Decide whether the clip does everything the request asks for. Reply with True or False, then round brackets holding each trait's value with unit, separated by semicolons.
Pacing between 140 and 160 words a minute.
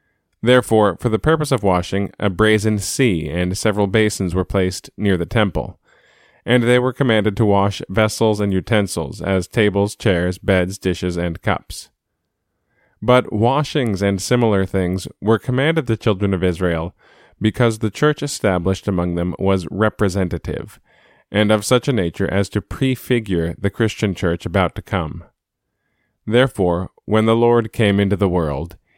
True (155 wpm)